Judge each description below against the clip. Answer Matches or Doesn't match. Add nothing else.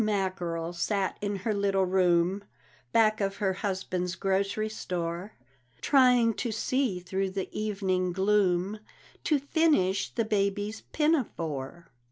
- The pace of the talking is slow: Matches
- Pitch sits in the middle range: Doesn't match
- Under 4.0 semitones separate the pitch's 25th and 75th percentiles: Matches